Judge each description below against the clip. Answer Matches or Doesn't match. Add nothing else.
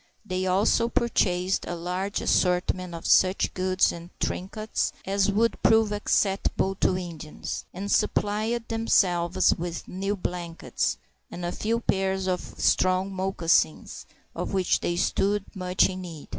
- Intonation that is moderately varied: Doesn't match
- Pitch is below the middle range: Doesn't match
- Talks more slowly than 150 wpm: Matches